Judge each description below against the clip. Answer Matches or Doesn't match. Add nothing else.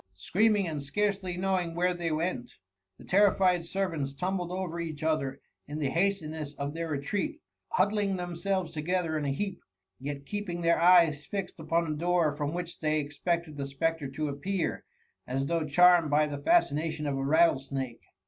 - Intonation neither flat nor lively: Matches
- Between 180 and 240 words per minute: Doesn't match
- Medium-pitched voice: Matches